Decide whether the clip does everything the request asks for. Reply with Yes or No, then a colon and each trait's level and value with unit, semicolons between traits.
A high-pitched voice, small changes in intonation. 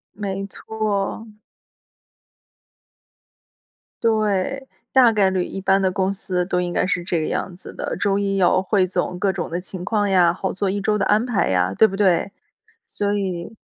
Yes: high, 195 Hz; narrow, 2.2 semitones